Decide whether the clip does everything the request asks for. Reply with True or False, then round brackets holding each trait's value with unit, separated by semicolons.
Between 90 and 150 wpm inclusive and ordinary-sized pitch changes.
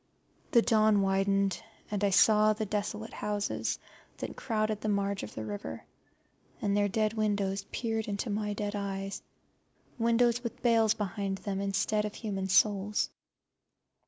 False (145 wpm; 1.6 semitones)